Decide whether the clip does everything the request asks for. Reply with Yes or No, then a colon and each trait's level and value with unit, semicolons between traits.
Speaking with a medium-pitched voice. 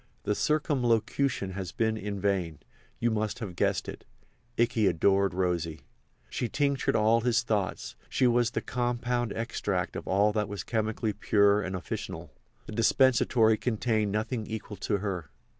No: low, 110 Hz